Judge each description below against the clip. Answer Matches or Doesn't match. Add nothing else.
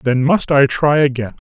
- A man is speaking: Matches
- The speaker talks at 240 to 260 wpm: Doesn't match